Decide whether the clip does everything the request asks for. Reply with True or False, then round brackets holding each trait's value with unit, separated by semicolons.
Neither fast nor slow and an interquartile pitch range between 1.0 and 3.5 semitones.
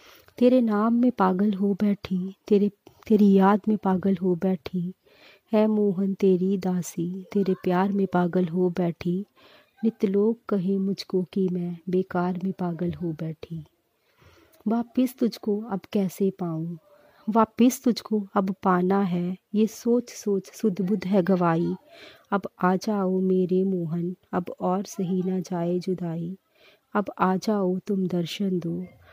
True (140 wpm; 2.4 semitones)